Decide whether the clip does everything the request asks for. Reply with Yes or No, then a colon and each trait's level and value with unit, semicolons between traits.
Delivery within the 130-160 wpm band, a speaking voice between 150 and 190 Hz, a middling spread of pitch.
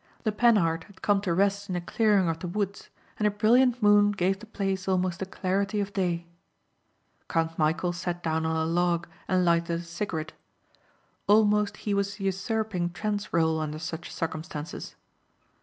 No: average, 170 wpm; medium, 185 Hz; average, 3.4 semitones